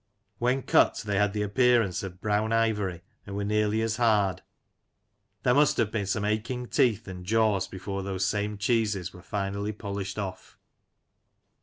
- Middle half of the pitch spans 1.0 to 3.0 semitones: Yes, narrow, 2.4 semitones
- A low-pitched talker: Yes, low, 105 Hz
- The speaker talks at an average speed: Yes, average, 160 wpm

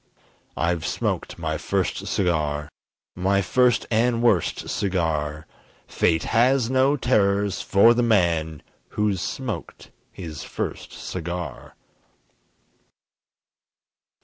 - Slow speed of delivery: Yes, slow, 95 wpm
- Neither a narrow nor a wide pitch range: No, wide, 5.7 semitones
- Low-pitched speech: Yes, low, 100 Hz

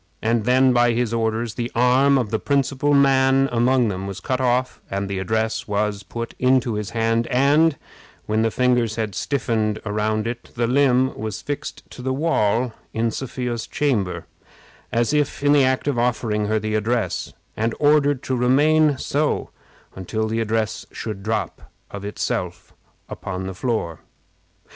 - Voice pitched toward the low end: Yes, low, 120 Hz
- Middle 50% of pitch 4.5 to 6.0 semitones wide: No, average, 3.4 semitones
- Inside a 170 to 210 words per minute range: No, average, 160 wpm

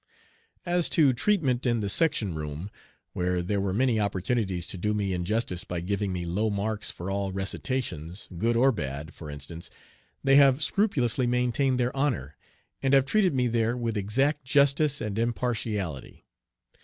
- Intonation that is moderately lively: No, wide, 6.0 semitones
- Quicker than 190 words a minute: No, average, 160 wpm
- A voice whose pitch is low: Yes, low, 110 Hz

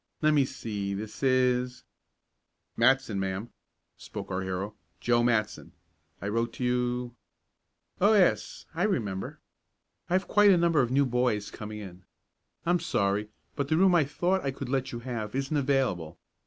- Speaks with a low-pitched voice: Yes, low, 125 Hz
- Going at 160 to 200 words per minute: Yes, average, 170 wpm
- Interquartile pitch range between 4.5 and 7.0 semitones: Yes, average, 5.1 semitones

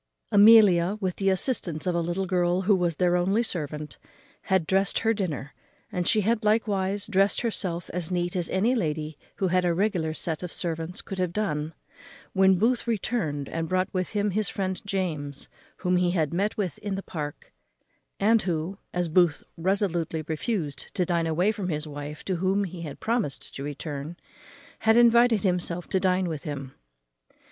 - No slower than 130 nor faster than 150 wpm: No, average, 180 wpm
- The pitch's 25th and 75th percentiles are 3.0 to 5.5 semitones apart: Yes, average, 3.5 semitones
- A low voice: No, medium, 180 Hz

